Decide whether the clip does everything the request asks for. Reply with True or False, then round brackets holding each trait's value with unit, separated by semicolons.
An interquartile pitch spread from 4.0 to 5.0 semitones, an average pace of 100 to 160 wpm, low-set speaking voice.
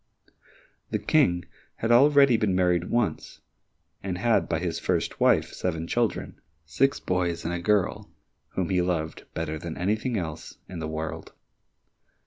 True (4.4 semitones; 145 wpm; 90 Hz)